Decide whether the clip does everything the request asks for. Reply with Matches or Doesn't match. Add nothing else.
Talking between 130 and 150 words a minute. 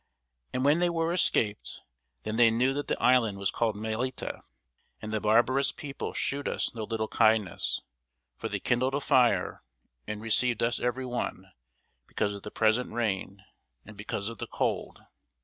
Doesn't match